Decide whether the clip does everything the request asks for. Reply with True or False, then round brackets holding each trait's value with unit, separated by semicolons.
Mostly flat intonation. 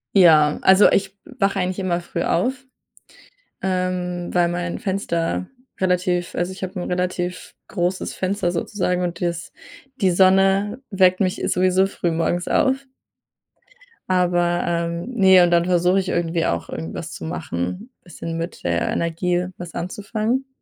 True (1.8 semitones)